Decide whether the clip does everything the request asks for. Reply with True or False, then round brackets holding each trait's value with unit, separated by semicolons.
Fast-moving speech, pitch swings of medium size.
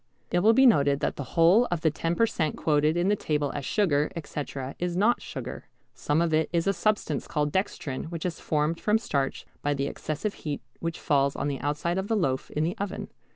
True (225 wpm; 4.3 semitones)